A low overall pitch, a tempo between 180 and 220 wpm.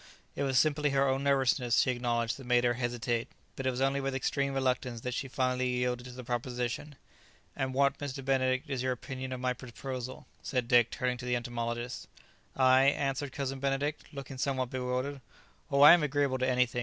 Yes: low, 130 Hz; average, 195 wpm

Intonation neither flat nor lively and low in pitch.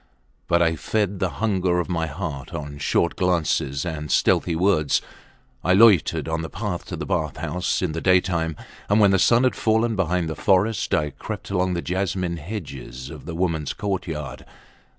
Yes: average, 3.4 semitones; very low, 90 Hz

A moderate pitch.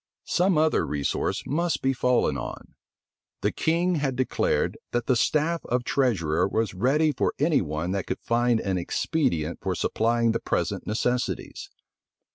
No: low, 125 Hz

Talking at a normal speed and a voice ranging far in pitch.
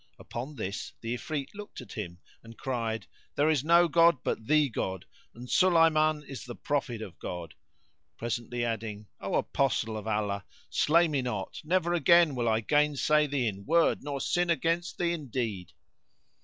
Yes: average, 170 wpm; wide, 5.7 semitones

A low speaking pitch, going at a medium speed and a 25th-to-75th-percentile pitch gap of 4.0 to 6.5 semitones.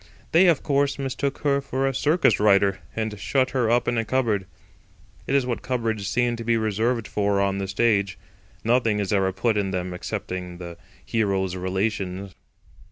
Yes: low, 110 Hz; average, 175 wpm; average, 4.5 semitones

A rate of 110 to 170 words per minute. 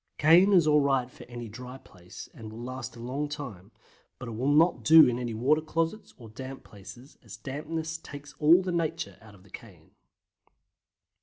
No: average, 190 wpm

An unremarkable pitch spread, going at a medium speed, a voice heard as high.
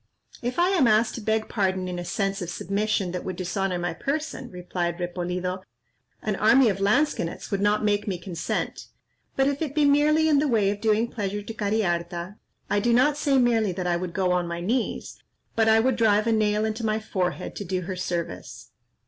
No: average, 4.2 semitones; fast, 210 wpm; high, 205 Hz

